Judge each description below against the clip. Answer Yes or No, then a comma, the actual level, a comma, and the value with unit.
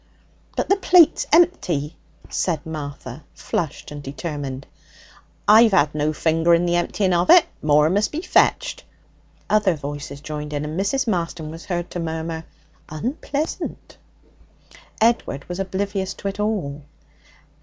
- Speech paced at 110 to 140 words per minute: Yes, slow, 135 wpm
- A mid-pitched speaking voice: Yes, medium, 170 Hz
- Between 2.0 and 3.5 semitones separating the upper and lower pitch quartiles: No, average, 5.2 semitones